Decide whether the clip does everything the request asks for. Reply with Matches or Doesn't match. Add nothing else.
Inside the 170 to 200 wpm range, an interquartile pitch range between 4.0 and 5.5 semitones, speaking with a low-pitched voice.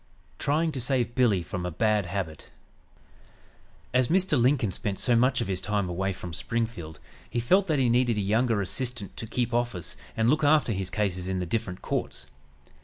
Matches